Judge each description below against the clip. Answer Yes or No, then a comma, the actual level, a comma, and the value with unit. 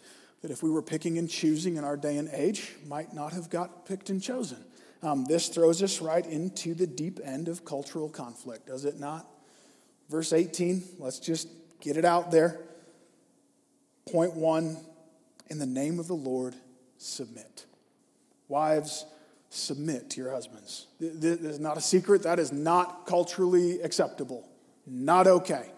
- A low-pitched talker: No, medium, 165 Hz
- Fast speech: No, average, 155 wpm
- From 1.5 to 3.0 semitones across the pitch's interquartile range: Yes, average, 2.7 semitones